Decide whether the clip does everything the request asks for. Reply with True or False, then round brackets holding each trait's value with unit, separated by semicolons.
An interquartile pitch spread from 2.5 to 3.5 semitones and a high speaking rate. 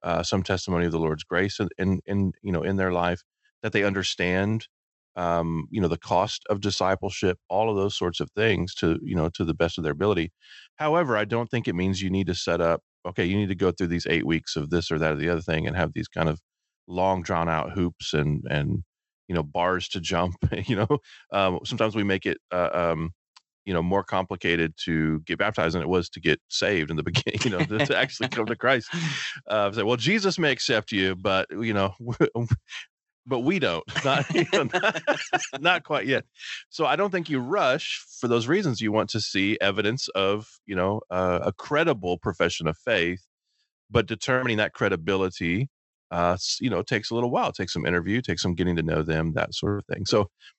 False (4.2 semitones; 215 wpm)